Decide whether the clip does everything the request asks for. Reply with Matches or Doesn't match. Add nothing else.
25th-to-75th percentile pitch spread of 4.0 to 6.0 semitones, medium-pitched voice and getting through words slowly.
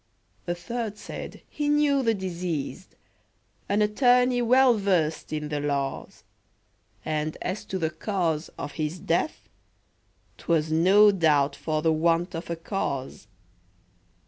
Matches